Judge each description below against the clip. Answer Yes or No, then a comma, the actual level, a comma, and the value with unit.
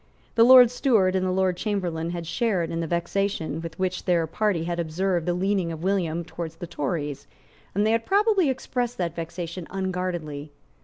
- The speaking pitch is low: No, medium, 180 Hz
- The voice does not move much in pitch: No, average, 3.3 semitones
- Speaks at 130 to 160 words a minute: No, average, 185 wpm